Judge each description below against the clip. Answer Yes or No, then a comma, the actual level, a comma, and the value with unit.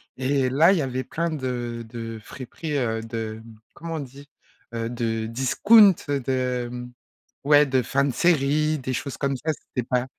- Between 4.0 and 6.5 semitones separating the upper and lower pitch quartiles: No, average, 3.2 semitones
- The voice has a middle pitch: No, low, 130 Hz